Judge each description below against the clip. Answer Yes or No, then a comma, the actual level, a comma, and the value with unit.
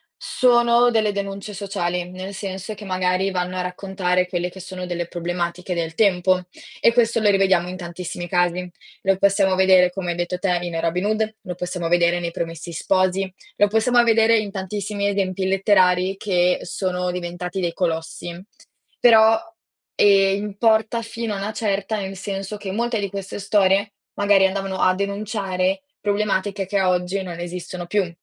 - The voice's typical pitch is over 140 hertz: Yes, high, 190 Hz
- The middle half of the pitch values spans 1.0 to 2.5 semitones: Yes, narrow, 2.2 semitones